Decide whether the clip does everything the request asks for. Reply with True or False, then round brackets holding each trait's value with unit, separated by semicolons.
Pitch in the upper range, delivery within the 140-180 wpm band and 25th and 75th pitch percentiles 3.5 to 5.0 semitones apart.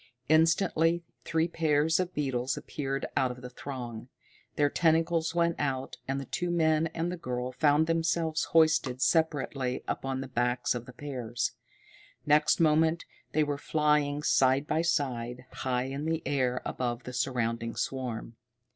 False (145 Hz; 150 wpm; 4.2 semitones)